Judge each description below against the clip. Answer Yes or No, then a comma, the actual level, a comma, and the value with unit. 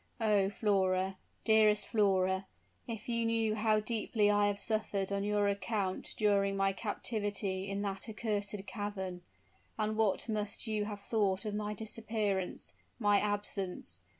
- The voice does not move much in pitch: Yes, narrow, 1.6 semitones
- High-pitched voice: Yes, high, 205 Hz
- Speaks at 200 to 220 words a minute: No, average, 140 wpm